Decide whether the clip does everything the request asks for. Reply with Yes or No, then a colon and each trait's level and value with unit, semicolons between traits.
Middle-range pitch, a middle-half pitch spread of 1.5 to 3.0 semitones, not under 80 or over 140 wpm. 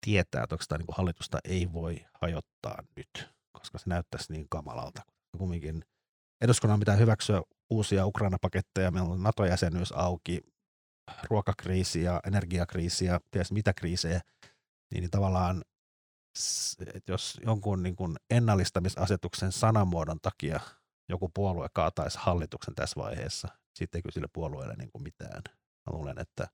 No: very low, 90 Hz; narrow, 2.6 semitones; average, 135 wpm